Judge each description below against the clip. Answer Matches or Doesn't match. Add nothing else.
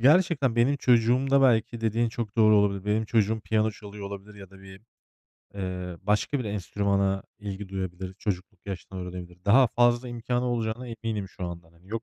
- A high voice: Doesn't match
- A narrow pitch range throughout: Doesn't match